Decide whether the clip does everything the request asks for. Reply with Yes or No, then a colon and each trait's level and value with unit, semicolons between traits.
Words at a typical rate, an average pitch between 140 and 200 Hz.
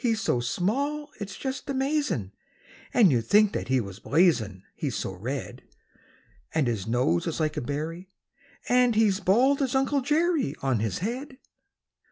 Yes: average, 170 wpm; high, 190 Hz